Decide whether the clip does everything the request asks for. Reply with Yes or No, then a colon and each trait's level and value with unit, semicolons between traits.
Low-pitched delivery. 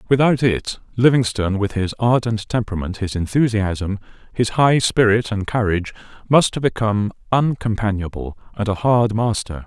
Yes: low, 110 Hz